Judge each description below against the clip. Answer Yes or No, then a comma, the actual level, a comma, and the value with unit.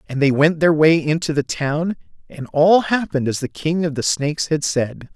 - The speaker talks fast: Yes, fast, 220 wpm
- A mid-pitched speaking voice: Yes, medium, 155 Hz